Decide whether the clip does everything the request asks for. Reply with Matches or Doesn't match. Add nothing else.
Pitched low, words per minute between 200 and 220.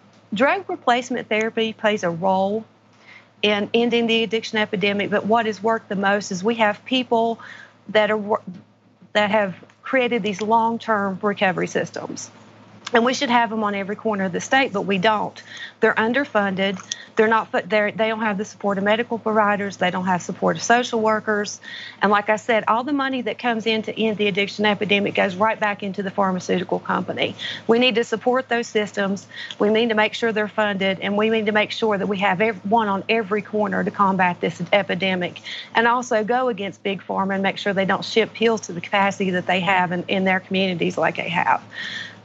Doesn't match